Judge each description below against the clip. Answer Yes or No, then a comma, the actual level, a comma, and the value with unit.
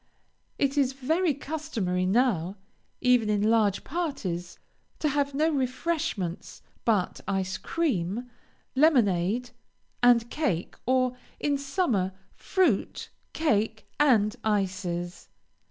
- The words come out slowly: Yes, slow, 100 wpm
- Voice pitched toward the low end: No, high, 240 Hz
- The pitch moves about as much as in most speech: No, wide, 6.6 semitones